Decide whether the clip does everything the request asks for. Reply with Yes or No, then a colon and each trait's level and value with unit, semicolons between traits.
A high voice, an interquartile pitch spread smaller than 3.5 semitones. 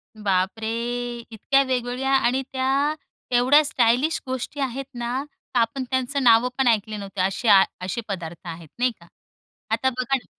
Yes: high, 245 Hz; average, 3.0 semitones